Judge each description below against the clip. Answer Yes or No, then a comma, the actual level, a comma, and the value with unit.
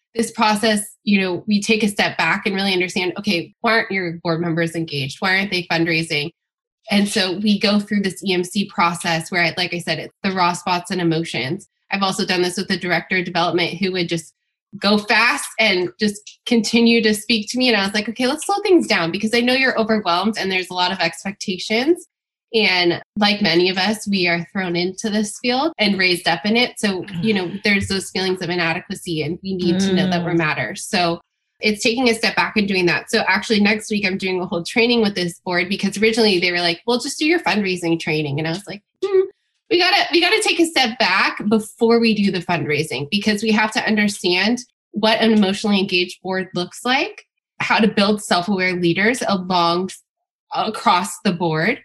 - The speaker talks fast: Yes, fast, 215 wpm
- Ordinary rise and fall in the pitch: Yes, average, 4.0 semitones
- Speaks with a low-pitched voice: No, high, 195 Hz